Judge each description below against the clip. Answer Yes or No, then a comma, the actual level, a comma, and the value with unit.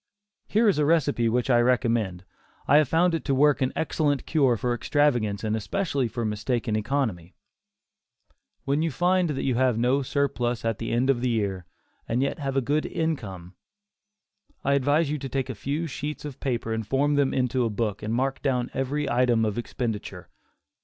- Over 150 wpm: Yes, average, 190 wpm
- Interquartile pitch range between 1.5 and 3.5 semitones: No, average, 4.0 semitones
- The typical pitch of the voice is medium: No, low, 130 Hz